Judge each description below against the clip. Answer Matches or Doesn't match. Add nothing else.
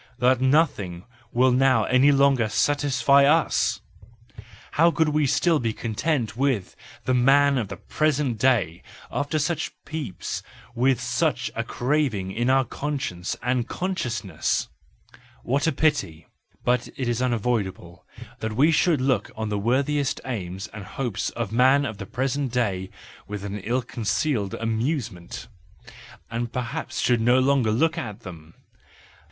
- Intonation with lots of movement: Doesn't match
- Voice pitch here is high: Doesn't match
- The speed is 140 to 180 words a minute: Matches